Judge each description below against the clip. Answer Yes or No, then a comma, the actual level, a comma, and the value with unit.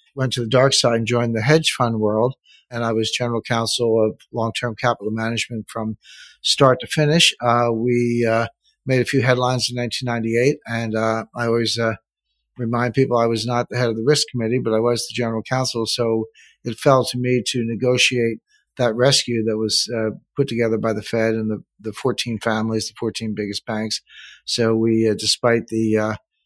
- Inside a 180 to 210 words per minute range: Yes, average, 200 wpm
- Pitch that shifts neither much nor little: No, narrow, 1.6 semitones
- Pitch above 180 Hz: No, low, 115 Hz